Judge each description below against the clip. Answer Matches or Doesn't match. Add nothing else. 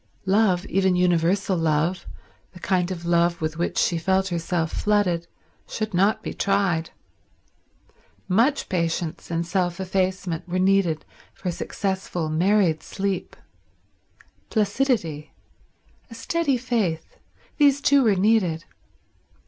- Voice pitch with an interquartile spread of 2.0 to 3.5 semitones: Matches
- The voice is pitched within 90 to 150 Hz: Doesn't match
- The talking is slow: Matches